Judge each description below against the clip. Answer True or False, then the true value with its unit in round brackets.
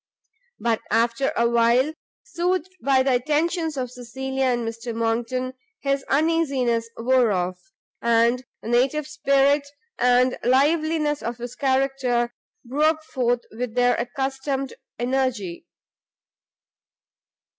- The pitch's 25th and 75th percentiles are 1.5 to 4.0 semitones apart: True (2.7 semitones)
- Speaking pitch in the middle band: False (255 Hz)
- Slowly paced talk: True (110 wpm)